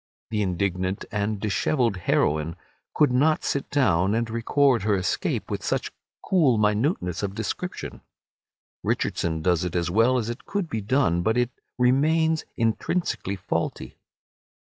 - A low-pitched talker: Yes, low, 110 Hz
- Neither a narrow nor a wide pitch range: No, wide, 5.8 semitones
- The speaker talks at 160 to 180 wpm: No, average, 140 wpm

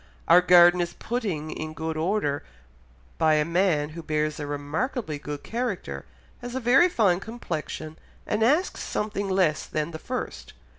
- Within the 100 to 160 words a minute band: Yes, average, 155 wpm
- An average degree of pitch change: No, wide, 5.7 semitones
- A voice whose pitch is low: No, medium, 170 Hz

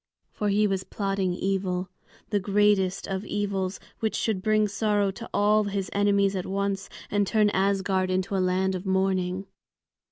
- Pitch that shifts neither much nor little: No, narrow, 1.5 semitones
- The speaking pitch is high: Yes, high, 195 Hz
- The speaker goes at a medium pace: Yes, average, 160 wpm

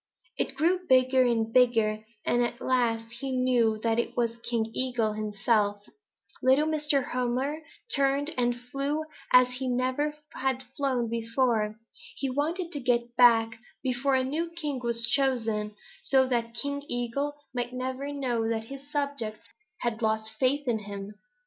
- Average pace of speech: Yes, average, 150 wpm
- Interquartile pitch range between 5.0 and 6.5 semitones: No, average, 3.1 semitones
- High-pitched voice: Yes, very high, 250 Hz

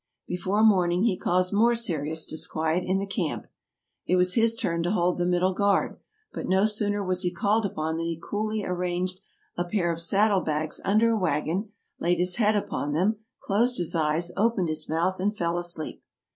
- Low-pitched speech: No, medium, 180 Hz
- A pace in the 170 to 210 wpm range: Yes, average, 190 wpm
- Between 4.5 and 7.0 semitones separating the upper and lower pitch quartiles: No, average, 3.3 semitones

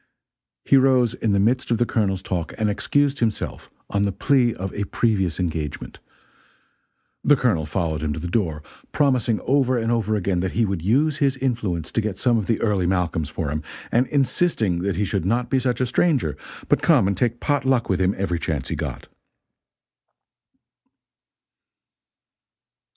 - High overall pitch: No, low, 105 Hz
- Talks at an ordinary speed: Yes, average, 180 wpm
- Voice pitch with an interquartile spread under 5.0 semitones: No, wide, 5.5 semitones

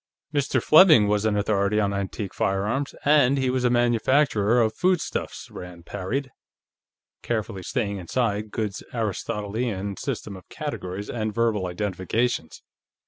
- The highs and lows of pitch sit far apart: No, average, 3.7 semitones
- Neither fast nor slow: No, slow, 130 wpm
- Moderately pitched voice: No, low, 105 Hz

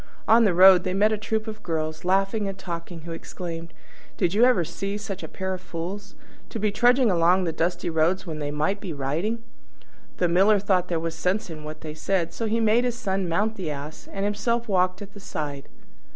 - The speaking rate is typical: No, fast, 220 wpm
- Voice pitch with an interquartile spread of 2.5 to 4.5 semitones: Yes, average, 4.0 semitones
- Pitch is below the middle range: No, medium, 185 Hz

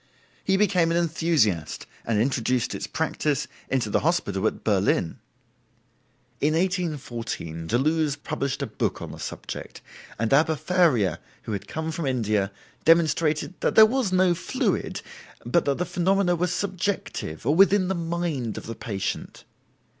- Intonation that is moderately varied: No, wide, 7.2 semitones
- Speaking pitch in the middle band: Yes, medium, 155 Hz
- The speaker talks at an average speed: Yes, average, 145 wpm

